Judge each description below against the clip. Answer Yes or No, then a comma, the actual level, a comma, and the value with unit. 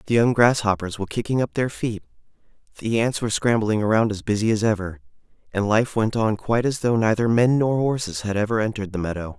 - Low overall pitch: Yes, low, 110 Hz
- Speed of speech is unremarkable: No, fast, 210 wpm